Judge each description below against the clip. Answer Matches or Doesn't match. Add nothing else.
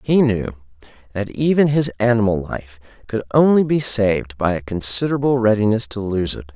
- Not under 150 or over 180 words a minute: Matches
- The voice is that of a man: Matches